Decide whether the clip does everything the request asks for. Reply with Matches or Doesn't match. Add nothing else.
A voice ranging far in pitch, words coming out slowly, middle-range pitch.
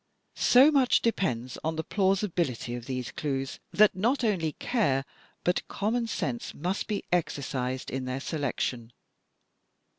Matches